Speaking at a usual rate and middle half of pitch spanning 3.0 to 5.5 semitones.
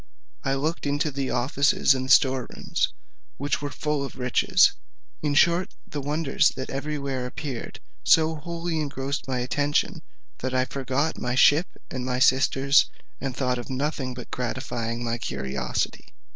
No: average, 150 wpm; narrow, 2.5 semitones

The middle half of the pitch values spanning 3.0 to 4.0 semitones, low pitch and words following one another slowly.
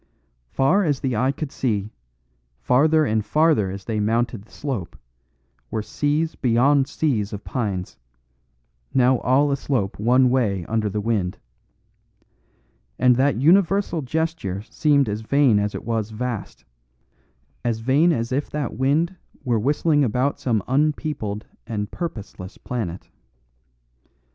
No: average, 5.3 semitones; low, 125 Hz; slow, 130 wpm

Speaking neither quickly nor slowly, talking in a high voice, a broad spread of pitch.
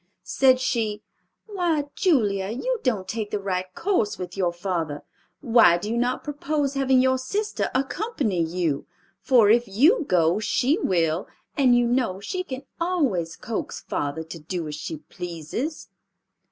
Yes: average, 155 wpm; high, 225 Hz; wide, 7.2 semitones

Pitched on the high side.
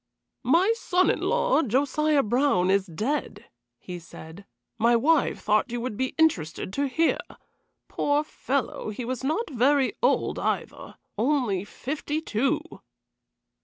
Yes: very high, 265 Hz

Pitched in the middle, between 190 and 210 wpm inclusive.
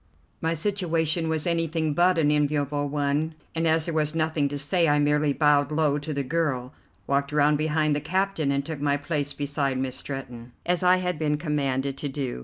Yes: medium, 150 Hz; average, 200 wpm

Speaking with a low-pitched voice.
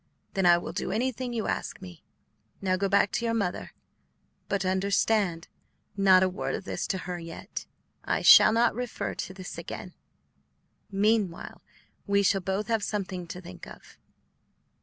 No: high, 195 Hz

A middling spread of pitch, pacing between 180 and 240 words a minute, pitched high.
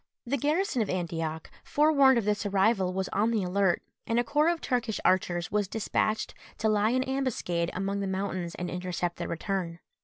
Yes: average, 4.8 semitones; average, 185 wpm; high, 200 Hz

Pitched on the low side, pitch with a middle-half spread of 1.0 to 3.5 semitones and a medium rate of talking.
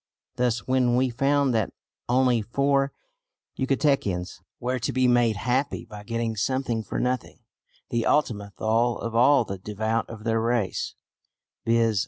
Yes: low, 120 Hz; narrow, 2.6 semitones; average, 145 wpm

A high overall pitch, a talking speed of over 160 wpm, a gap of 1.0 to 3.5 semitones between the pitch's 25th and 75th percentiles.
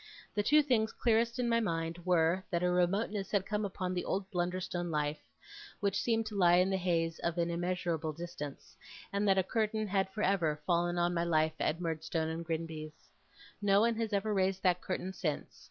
No: medium, 180 Hz; average, 200 wpm; average, 3.2 semitones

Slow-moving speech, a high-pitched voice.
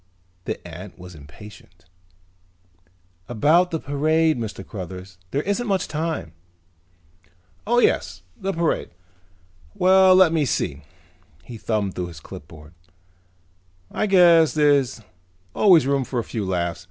No: slow, 125 wpm; low, 135 Hz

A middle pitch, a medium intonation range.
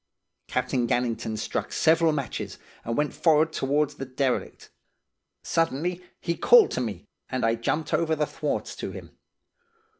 Yes: medium, 145 Hz; average, 4.5 semitones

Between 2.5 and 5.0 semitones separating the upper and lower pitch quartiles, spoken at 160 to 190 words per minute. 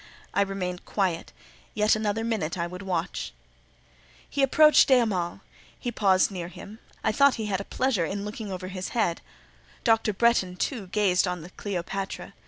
Yes: average, 3.4 semitones; average, 170 wpm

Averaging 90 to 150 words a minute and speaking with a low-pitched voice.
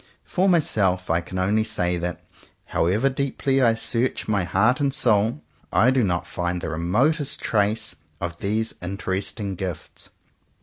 Yes: average, 145 wpm; low, 105 Hz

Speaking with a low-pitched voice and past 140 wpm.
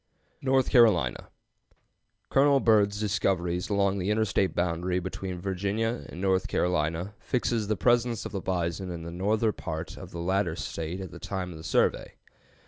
Yes: very low, 95 Hz; average, 160 wpm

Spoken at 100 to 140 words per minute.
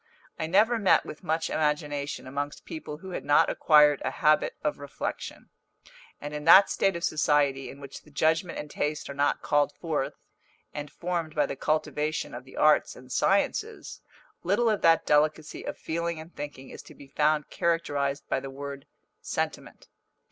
No: average, 175 wpm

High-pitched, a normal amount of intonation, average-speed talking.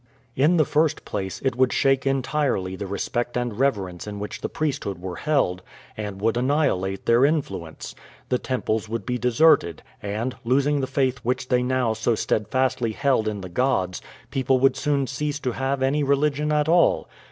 No: low, 125 Hz; average, 4.8 semitones; average, 175 wpm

